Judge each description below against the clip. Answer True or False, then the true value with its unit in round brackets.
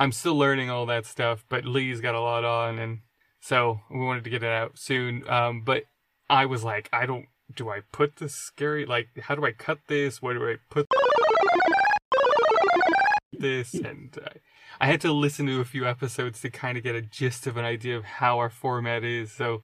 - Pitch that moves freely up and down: False (3.5 semitones)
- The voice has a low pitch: True (130 Hz)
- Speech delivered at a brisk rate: True (210 wpm)